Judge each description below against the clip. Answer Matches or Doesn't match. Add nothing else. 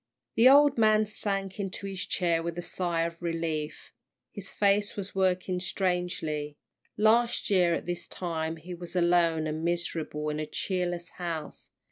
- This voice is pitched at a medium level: Matches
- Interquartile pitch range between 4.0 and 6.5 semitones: Doesn't match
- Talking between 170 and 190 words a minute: Doesn't match